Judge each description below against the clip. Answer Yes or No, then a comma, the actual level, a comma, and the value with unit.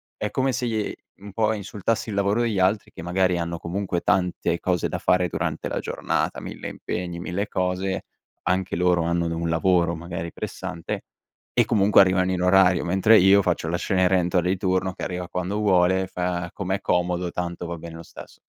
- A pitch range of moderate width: No, narrow, 1.8 semitones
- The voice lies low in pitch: Yes, very low, 90 Hz